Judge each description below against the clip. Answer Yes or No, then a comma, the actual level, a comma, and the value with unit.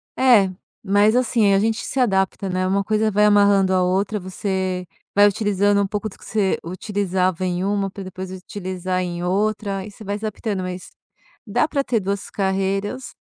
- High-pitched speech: Yes, high, 195 Hz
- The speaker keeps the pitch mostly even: Yes, narrow, 2.0 semitones